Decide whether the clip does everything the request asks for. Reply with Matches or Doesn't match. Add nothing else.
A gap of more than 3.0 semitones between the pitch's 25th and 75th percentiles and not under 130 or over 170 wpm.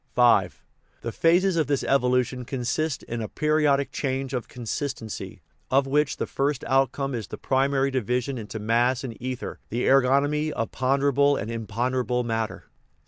Doesn't match